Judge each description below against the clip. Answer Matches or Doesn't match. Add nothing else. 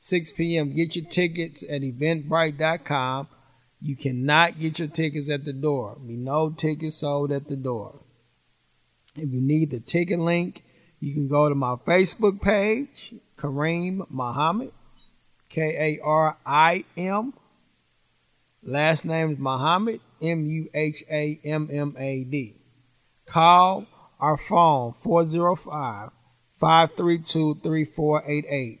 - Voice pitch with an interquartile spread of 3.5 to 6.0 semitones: Doesn't match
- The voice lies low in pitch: Doesn't match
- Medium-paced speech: Doesn't match